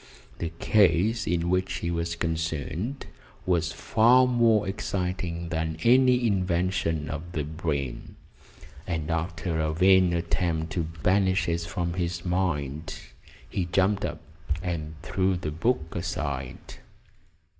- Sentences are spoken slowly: Yes, slow, 125 wpm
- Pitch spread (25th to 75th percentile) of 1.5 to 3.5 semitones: Yes, narrow, 2.6 semitones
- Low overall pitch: Yes, very low, 85 Hz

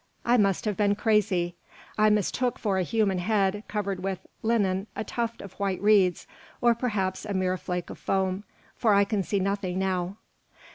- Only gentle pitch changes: Yes, narrow, 2.3 semitones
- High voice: Yes, high, 200 Hz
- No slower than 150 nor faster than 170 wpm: No, average, 180 wpm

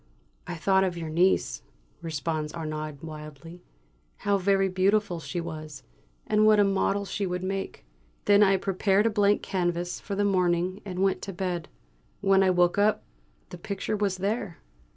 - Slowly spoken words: No, average, 165 wpm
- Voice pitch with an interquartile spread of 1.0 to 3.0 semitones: Yes, average, 2.7 semitones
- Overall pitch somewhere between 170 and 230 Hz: Yes, medium, 185 Hz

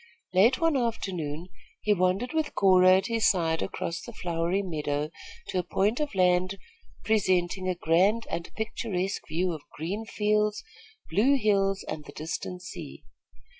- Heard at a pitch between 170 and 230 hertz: Yes, medium, 185 Hz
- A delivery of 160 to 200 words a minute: No, average, 150 wpm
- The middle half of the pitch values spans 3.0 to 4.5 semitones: Yes, average, 3.5 semitones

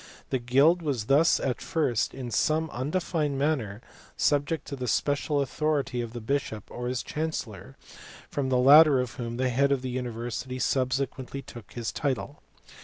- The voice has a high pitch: No, low, 130 Hz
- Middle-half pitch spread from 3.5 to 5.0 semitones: No, average, 2.9 semitones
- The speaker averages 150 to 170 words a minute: Yes, average, 165 wpm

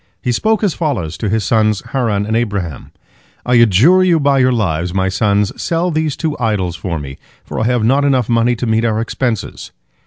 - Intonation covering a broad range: No, average, 5.0 semitones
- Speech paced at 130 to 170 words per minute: No, fast, 205 wpm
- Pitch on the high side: No, low, 115 Hz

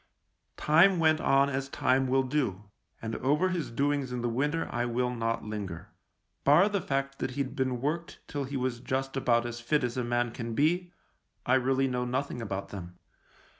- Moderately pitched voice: No, low, 130 Hz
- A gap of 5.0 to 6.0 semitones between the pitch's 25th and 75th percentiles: No, average, 3.1 semitones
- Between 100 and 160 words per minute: No, average, 190 wpm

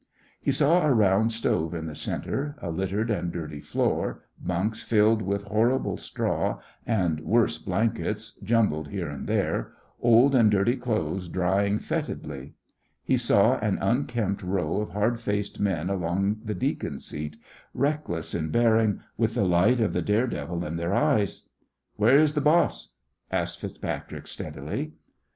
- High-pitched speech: No, low, 105 Hz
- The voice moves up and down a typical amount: Yes, average, 4.7 semitones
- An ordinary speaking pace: Yes, average, 150 wpm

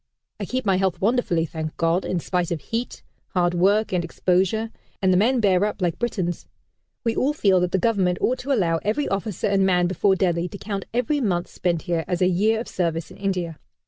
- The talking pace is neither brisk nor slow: No, fast, 215 wpm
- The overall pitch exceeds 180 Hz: Yes, high, 190 Hz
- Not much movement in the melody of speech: No, average, 3.7 semitones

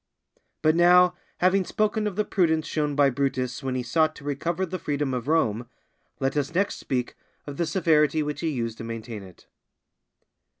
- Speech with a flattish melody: No, average, 5.1 semitones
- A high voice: No, medium, 150 Hz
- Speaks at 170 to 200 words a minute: Yes, average, 180 wpm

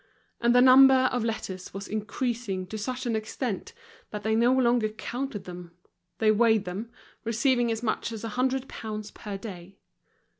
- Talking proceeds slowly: No, average, 165 wpm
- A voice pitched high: Yes, high, 225 Hz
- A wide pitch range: No, average, 3.0 semitones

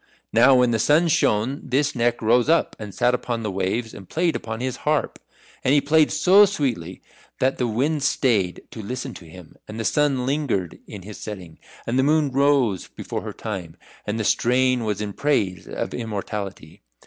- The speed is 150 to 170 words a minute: No, average, 190 wpm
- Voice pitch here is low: Yes, low, 120 Hz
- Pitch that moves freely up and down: No, average, 5.0 semitones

